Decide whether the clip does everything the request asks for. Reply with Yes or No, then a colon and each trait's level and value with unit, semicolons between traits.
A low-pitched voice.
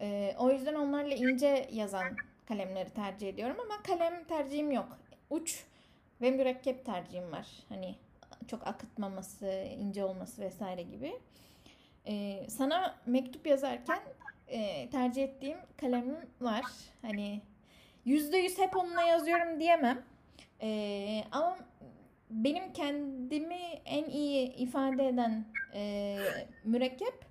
No: very high, 260 Hz